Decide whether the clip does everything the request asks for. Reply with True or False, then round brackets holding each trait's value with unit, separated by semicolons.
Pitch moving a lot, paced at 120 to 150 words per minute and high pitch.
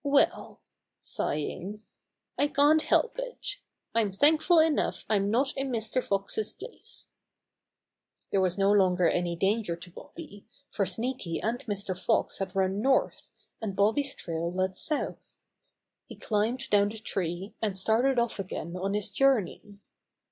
True (5.8 semitones; 140 wpm; 210 Hz)